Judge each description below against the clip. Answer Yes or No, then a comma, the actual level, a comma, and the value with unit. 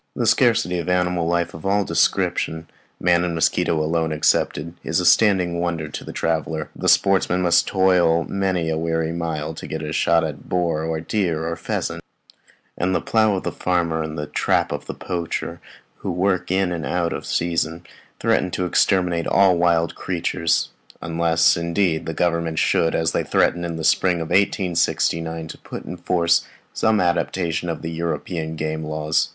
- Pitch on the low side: Yes, very low, 85 Hz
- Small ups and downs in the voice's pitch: Yes, narrow, 1.7 semitones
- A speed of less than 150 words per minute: No, average, 175 wpm